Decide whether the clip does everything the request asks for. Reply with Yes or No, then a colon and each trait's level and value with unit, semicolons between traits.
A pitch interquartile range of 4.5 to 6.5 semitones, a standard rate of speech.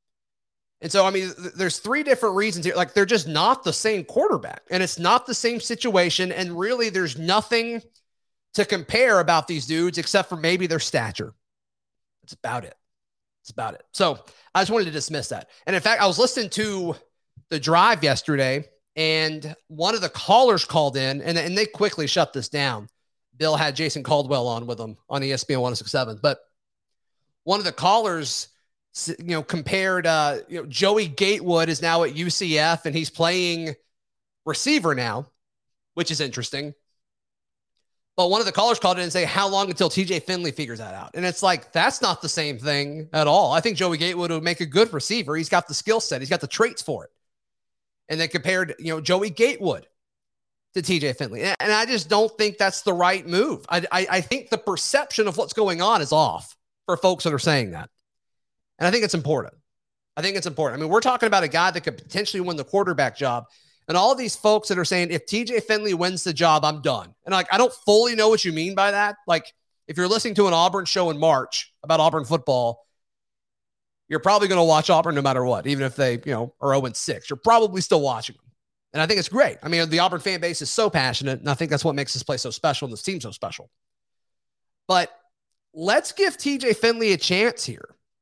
No: average, 4.9 semitones; fast, 215 wpm